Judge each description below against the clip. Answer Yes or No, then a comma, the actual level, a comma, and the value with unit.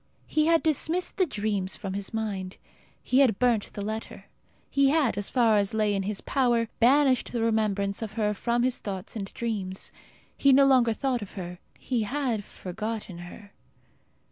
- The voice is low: No, high, 220 Hz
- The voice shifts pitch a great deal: No, average, 4.2 semitones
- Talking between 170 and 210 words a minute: Yes, average, 175 wpm